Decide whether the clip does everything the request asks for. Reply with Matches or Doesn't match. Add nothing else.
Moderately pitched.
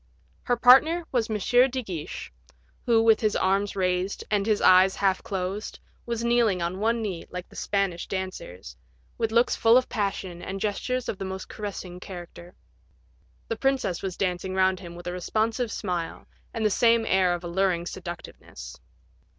Doesn't match